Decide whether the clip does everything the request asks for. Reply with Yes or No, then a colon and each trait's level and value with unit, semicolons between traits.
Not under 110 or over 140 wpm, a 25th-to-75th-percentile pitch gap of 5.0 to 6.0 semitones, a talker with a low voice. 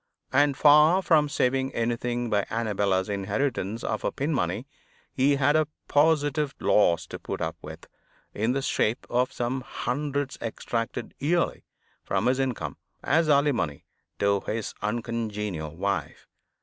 Yes: slow, 135 wpm; average, 5.3 semitones; low, 125 Hz